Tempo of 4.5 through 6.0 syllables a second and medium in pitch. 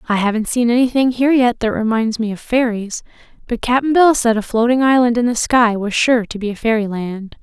No: 5.5 syllables/s; high, 235 Hz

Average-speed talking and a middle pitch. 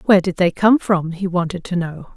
No: fast, 250 wpm; medium, 180 Hz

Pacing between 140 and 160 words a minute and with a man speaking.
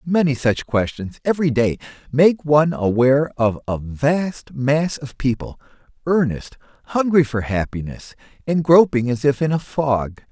Yes: average, 145 wpm; male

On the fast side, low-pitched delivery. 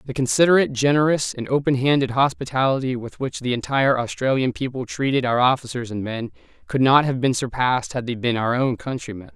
No: average, 185 wpm; low, 130 Hz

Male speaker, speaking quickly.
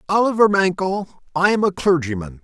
No: male; average, 150 wpm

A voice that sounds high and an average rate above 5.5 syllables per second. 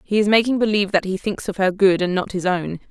Yes: high, 195 Hz; 6.3 syllables/s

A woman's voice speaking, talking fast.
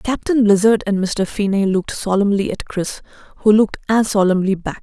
No: female; average, 175 wpm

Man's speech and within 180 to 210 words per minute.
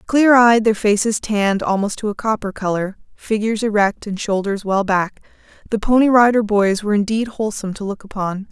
No: female; average, 185 wpm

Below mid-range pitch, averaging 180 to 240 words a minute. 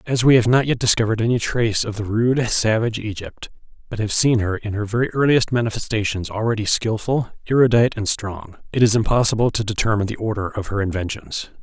Yes: low, 110 Hz; average, 190 wpm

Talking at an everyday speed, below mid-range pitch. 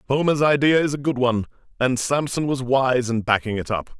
No: fast, 210 wpm; low, 130 Hz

